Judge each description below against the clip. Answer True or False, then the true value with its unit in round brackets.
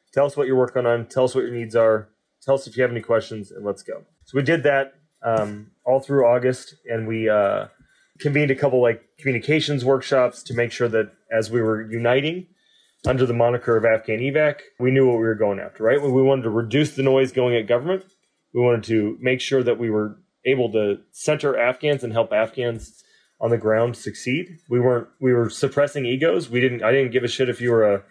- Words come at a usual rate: False (230 wpm)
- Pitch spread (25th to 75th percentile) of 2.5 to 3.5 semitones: True (3.0 semitones)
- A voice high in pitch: False (125 Hz)